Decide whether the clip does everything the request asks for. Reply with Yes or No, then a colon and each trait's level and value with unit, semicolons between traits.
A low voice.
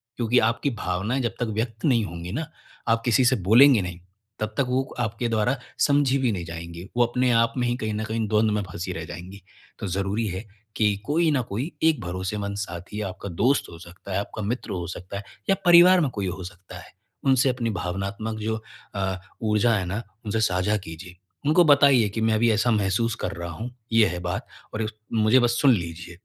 Yes: low, 110 Hz